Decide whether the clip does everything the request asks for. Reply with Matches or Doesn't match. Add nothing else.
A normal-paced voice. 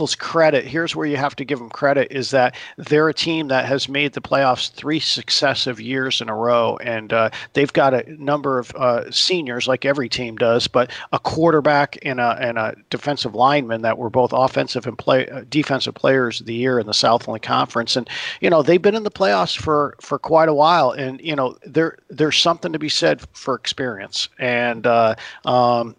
Doesn't match